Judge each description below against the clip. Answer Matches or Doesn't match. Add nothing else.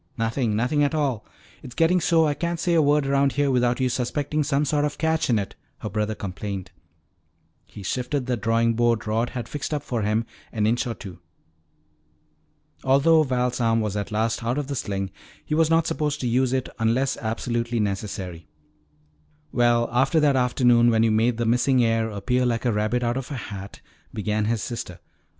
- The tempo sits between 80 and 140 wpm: Doesn't match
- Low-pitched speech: Matches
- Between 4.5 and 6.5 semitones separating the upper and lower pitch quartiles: Doesn't match